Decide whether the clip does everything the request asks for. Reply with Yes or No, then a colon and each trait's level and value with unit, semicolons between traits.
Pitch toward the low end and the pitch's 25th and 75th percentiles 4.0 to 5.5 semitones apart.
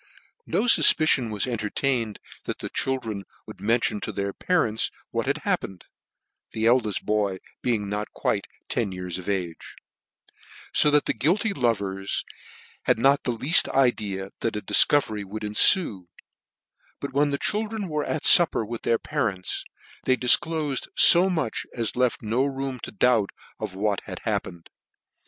Yes: low, 115 Hz; average, 5.2 semitones